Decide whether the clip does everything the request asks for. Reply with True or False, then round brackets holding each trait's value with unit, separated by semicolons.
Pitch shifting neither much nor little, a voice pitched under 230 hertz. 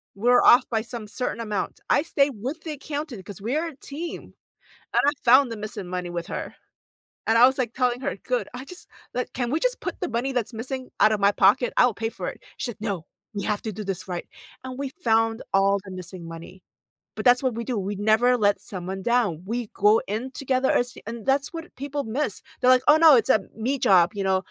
False (4.4 semitones; 235 Hz)